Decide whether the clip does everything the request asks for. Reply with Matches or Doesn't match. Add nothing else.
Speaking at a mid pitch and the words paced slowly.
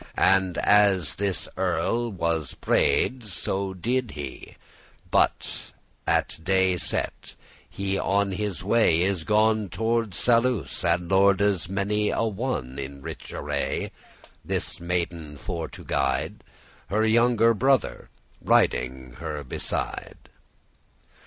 Doesn't match